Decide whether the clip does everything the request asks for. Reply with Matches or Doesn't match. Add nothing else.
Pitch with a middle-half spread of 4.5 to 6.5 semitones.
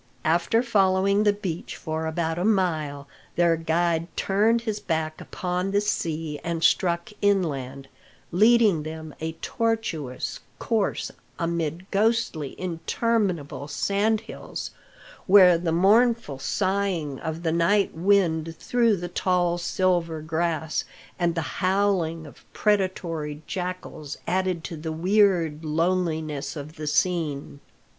Doesn't match